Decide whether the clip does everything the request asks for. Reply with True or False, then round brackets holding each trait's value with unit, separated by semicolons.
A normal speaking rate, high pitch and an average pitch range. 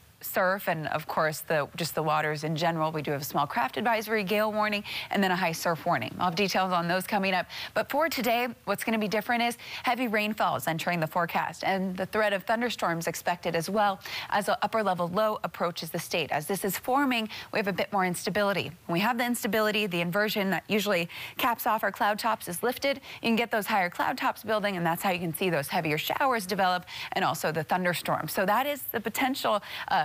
False (230 wpm; 195 Hz; 4.2 semitones)